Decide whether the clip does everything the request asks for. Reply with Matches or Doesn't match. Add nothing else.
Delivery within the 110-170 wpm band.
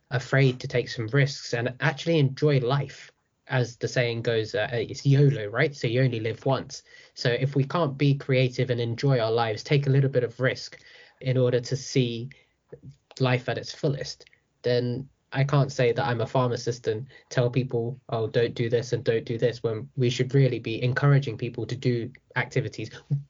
Doesn't match